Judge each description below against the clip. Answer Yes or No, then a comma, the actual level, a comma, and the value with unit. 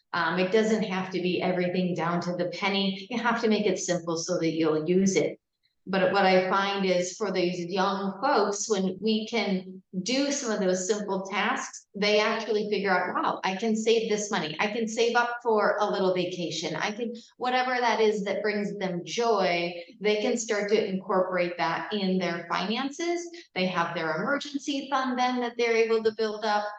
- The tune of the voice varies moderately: Yes, average, 3.6 semitones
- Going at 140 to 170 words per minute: No, average, 195 wpm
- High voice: Yes, high, 205 Hz